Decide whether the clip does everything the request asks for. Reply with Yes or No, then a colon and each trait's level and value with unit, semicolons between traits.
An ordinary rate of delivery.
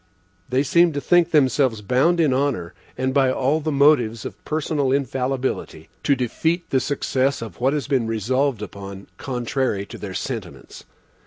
Yes: average, 160 wpm